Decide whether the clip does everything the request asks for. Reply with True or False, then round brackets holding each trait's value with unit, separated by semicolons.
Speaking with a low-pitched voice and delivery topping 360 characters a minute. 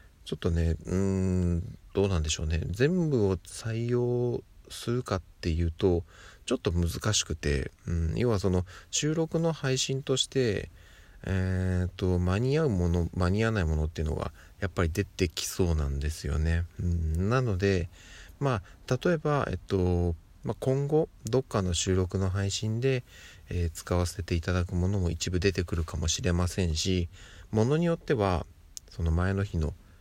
False (95 Hz; 315 characters per minute)